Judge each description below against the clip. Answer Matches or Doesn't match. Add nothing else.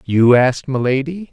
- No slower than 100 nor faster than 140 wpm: Matches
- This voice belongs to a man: Matches